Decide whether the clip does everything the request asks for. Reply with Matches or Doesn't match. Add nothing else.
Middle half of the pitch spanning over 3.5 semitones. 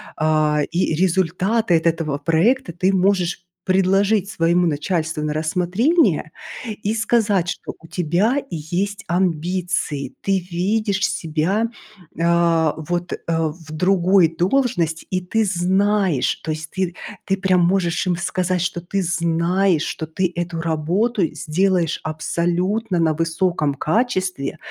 Doesn't match